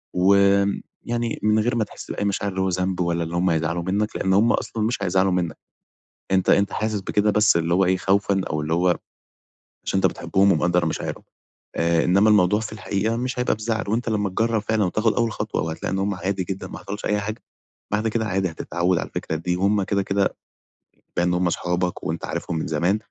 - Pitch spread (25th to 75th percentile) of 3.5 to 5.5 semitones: No, average, 3.1 semitones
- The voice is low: Yes, very low, 95 Hz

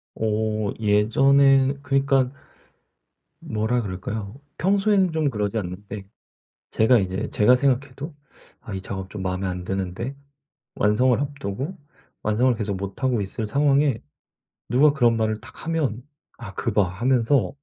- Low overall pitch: Yes, low, 115 Hz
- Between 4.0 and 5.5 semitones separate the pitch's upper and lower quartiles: Yes, average, 5.1 semitones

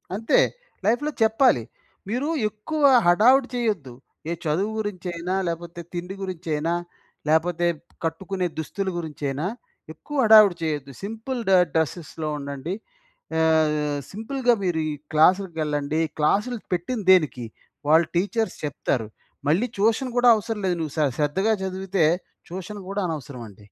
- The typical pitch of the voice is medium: Yes, medium, 175 Hz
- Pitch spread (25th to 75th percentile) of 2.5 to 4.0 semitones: No, average, 5.3 semitones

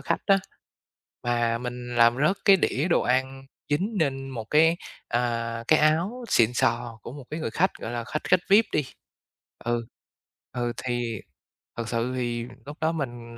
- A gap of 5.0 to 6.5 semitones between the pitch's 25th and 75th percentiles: No, average, 4.6 semitones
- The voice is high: No, low, 125 Hz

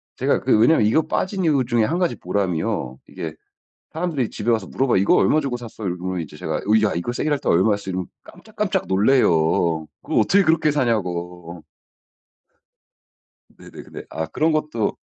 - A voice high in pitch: No, low, 110 Hz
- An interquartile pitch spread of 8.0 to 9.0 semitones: Yes, wide, 8.6 semitones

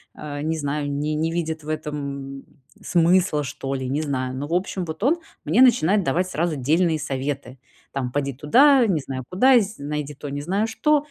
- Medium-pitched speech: Yes, medium, 150 Hz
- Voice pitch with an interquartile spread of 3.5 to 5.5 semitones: Yes, average, 4.5 semitones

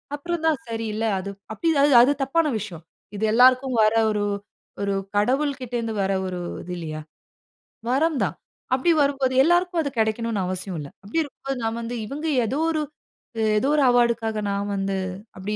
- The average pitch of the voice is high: Yes, high, 235 Hz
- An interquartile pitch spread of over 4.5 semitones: Yes, wide, 5.4 semitones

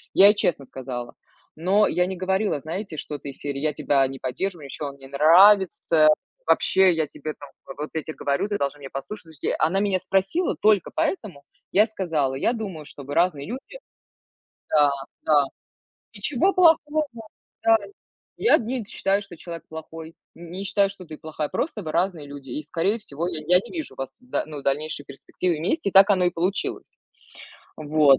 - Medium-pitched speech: Yes, medium, 170 Hz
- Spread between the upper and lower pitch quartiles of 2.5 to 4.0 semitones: No, average, 5.2 semitones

